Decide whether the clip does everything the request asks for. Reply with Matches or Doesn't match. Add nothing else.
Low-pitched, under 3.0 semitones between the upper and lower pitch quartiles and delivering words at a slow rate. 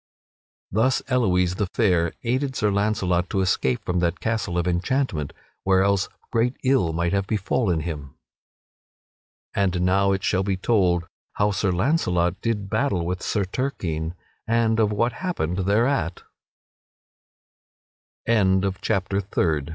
Doesn't match